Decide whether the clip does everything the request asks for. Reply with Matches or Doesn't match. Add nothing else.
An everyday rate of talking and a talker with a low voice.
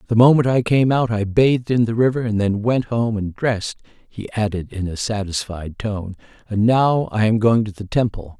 Doesn't match